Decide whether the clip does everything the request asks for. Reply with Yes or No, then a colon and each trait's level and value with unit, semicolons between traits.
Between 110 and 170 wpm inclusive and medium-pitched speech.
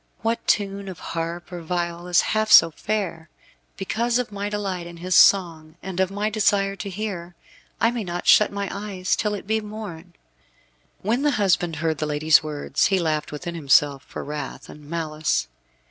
No: average, 180 wpm; medium, 180 Hz